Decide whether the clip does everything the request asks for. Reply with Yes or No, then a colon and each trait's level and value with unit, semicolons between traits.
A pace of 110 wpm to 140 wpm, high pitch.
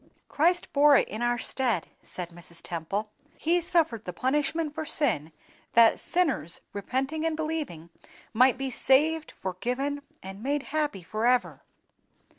Yes: slow, 135 wpm; very high, 260 Hz